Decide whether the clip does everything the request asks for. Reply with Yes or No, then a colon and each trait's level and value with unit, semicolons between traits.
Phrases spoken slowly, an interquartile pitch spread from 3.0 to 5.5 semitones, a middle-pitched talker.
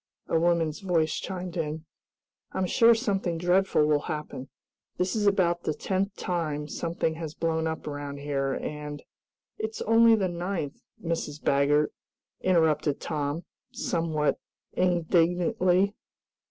Yes: slow, 125 wpm; average, 3.6 semitones; medium, 165 Hz